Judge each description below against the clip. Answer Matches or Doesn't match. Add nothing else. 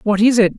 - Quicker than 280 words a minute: Matches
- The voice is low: Doesn't match